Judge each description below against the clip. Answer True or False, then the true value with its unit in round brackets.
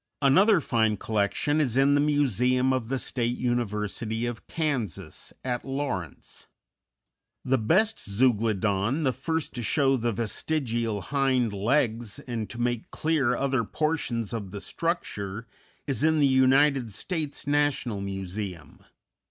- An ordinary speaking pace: False (130 wpm)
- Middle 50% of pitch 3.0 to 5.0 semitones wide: True (4.6 semitones)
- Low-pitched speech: True (125 Hz)